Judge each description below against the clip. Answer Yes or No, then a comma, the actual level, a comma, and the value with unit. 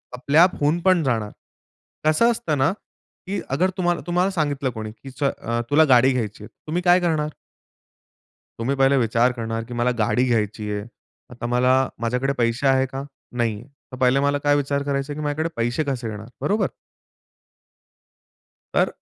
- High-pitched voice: No, low, 135 Hz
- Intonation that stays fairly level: No, average, 4.3 semitones